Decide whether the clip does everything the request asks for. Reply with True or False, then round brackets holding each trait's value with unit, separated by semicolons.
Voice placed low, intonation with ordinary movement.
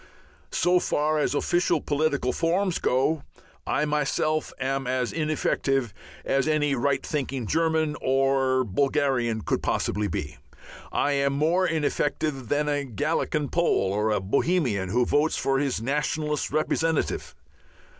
False (145 Hz; 3.0 semitones)